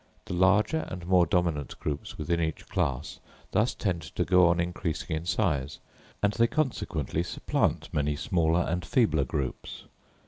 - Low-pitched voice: Yes, very low, 85 Hz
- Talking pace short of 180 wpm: Yes, average, 150 wpm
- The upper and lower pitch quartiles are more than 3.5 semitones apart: No, average, 3.2 semitones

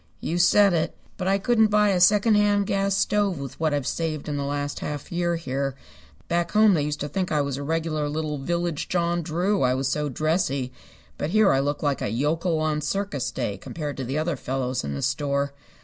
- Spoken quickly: Yes, fast, 215 wpm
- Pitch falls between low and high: Yes, medium, 155 Hz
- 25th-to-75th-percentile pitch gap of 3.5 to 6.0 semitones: Yes, average, 4.3 semitones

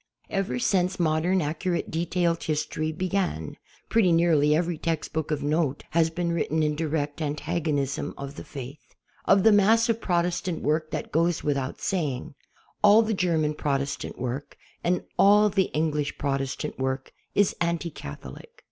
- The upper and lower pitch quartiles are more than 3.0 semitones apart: Yes, average, 3.4 semitones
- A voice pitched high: No, medium, 160 Hz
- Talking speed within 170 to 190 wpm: No, average, 155 wpm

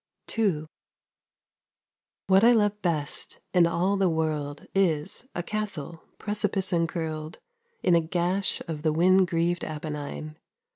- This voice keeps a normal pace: No, slow, 130 wpm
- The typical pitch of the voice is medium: Yes, medium, 170 Hz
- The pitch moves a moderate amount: Yes, average, 3.6 semitones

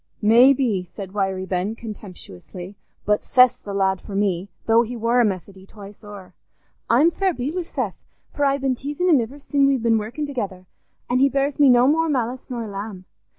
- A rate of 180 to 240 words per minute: Yes, average, 195 wpm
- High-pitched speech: Yes, high, 230 Hz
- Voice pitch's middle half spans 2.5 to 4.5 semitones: No, wide, 5.6 semitones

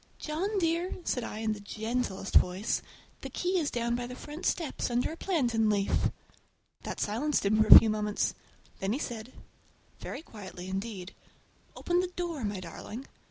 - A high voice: Yes, high, 235 Hz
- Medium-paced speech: Yes, average, 165 wpm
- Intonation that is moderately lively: No, wide, 6.6 semitones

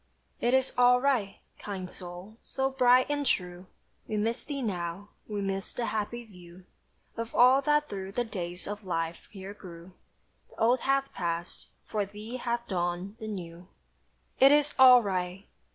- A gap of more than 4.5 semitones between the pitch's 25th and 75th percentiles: Yes, wide, 5.4 semitones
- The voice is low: No, high, 210 Hz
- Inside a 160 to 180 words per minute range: Yes, average, 165 wpm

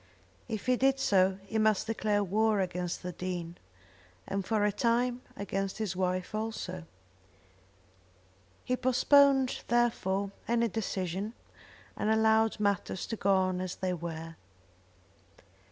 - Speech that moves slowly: Yes, slow, 125 wpm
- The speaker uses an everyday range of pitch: Yes, average, 3.4 semitones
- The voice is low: No, high, 205 Hz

